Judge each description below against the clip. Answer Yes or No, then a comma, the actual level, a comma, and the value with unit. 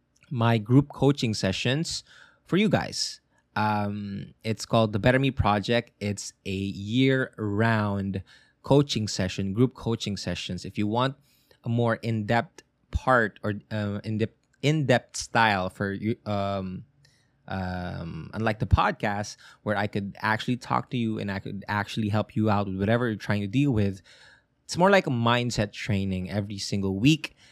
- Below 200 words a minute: Yes, average, 160 wpm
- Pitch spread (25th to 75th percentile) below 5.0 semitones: Yes, average, 3.6 semitones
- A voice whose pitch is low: Yes, low, 110 Hz